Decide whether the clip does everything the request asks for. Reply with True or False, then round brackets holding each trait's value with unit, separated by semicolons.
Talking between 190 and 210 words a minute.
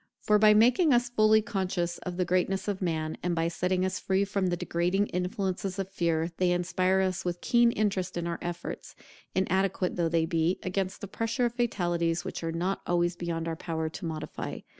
True (200 wpm)